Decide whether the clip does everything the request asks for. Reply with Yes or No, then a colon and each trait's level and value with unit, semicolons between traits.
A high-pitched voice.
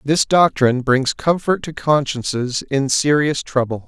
No: medium, 140 Hz